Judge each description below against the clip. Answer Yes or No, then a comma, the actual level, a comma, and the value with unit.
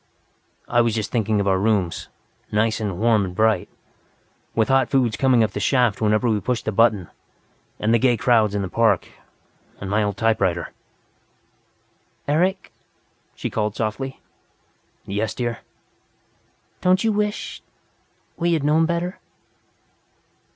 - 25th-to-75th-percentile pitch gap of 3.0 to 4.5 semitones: Yes, average, 4.1 semitones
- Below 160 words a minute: Yes, average, 140 wpm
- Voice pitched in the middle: No, low, 110 Hz